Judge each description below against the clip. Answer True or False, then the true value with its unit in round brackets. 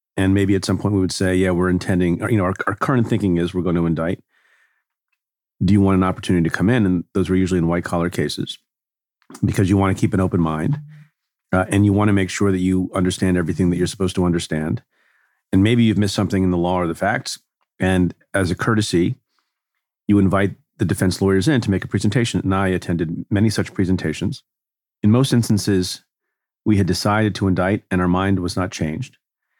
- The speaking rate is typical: False (220 wpm)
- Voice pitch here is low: True (95 Hz)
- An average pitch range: False (2.2 semitones)